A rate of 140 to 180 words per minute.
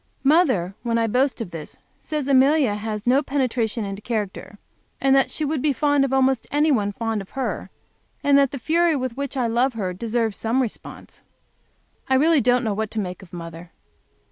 No: average, 195 wpm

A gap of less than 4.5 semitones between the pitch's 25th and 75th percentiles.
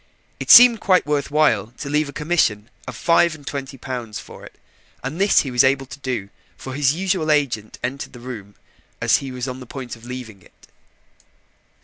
Yes: average, 3.5 semitones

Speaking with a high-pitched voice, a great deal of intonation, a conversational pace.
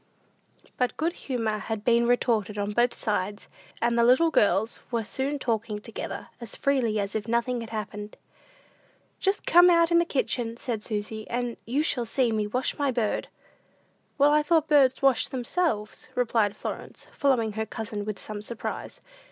No: high, 235 Hz; average, 3.7 semitones; average, 170 wpm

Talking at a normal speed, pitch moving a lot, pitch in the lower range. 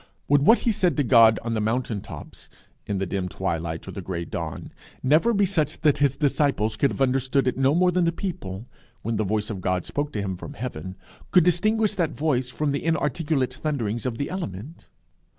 No: fast, 210 wpm; wide, 7.0 semitones; low, 130 Hz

